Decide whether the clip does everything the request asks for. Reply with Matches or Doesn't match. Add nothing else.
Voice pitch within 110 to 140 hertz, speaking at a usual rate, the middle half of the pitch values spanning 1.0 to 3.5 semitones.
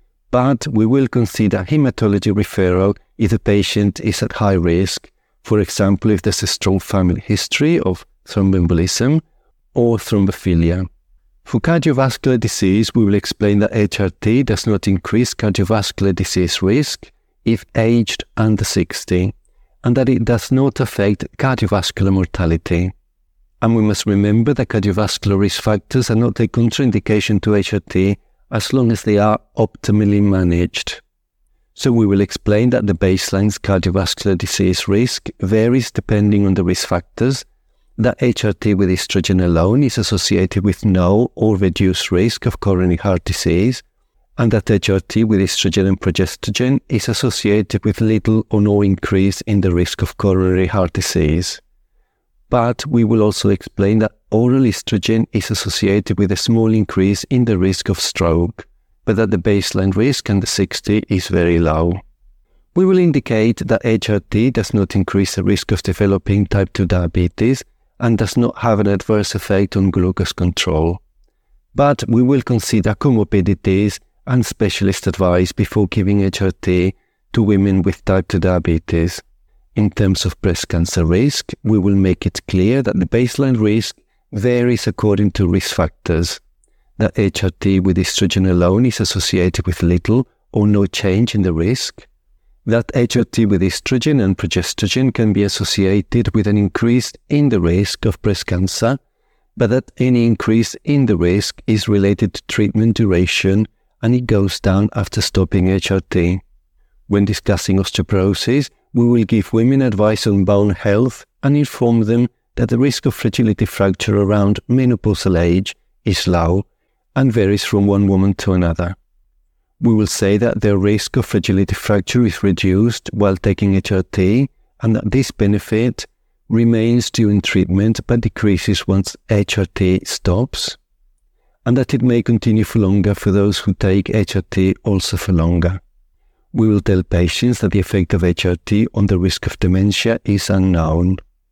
Doesn't match